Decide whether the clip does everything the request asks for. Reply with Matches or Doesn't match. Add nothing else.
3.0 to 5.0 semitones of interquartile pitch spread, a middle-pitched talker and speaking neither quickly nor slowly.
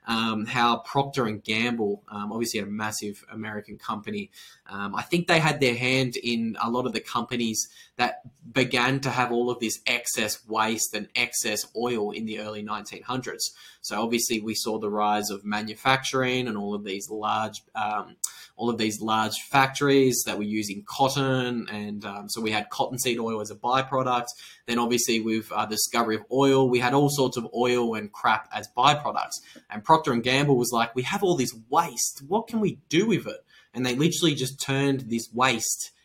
Doesn't match